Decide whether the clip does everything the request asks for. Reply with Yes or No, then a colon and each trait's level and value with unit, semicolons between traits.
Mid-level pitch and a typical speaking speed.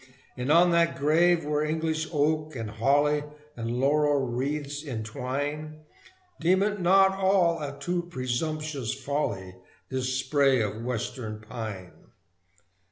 No: medium, 145 Hz; slow, 120 wpm